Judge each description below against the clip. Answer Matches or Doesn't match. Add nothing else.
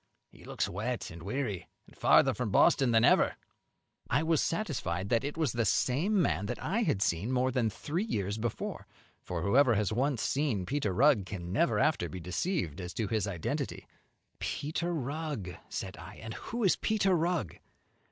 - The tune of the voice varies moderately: Doesn't match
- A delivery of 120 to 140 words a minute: Doesn't match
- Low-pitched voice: Matches